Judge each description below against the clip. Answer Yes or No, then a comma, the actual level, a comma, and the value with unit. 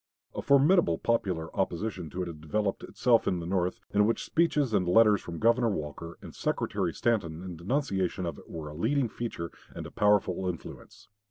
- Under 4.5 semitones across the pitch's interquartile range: No, wide, 5.5 semitones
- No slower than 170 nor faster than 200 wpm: Yes, average, 185 wpm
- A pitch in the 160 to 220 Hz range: No, very low, 95 Hz